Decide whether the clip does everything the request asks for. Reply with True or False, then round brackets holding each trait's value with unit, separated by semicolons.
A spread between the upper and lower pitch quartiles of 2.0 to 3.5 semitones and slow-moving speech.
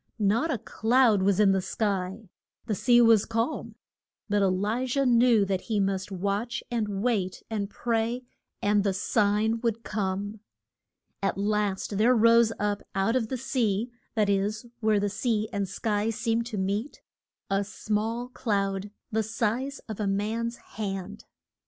False (2.6 semitones; 160 wpm)